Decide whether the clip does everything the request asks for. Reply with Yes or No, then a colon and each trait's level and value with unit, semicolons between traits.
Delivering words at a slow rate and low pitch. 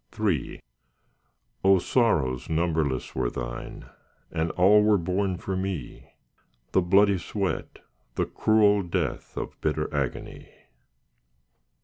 Yes: slow, 105 wpm; very low, 90 Hz